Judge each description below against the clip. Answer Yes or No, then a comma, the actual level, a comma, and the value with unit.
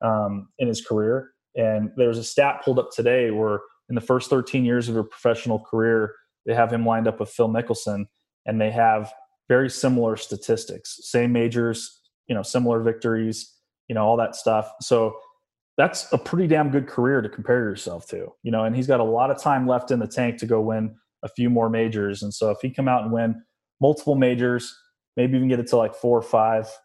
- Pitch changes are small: Yes, narrow, 2.3 semitones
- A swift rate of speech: Yes, fast, 215 wpm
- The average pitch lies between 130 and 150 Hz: No, low, 115 Hz